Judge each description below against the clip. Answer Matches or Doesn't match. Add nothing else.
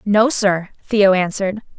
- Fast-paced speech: Doesn't match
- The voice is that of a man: Doesn't match